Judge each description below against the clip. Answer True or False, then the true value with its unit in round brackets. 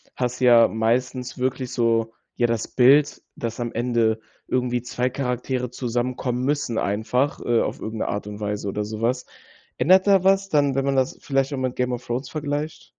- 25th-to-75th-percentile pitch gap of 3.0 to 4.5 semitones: False (2.6 semitones)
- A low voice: True (125 Hz)